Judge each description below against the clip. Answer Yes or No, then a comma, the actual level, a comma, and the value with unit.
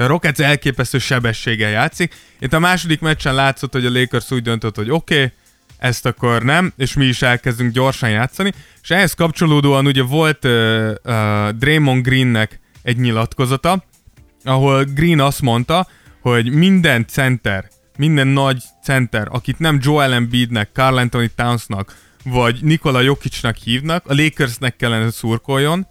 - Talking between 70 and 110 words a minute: No, average, 145 wpm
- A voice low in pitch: Yes, low, 130 Hz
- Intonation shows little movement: No, average, 3.7 semitones